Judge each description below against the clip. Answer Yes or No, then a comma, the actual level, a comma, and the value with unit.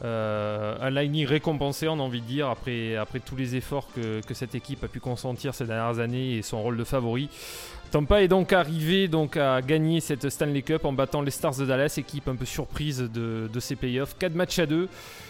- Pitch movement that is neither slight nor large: Yes, average, 3.9 semitones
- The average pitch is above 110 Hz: Yes, low, 135 Hz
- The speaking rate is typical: No, fast, 225 wpm